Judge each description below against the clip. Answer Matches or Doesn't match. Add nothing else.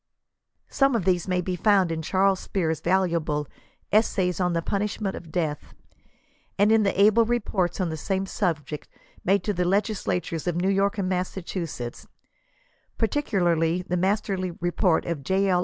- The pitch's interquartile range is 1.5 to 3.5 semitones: Matches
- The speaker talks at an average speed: Matches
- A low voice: Doesn't match